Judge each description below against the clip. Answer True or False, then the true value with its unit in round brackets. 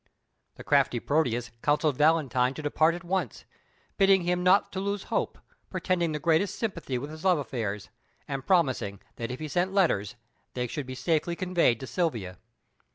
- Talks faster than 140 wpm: True (170 wpm)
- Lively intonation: True (5.8 semitones)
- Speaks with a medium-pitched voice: True (155 Hz)